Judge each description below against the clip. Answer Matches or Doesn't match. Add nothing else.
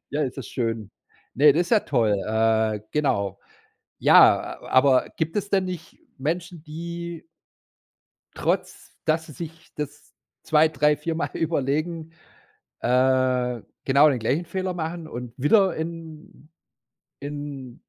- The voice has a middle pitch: Matches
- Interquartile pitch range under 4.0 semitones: Doesn't match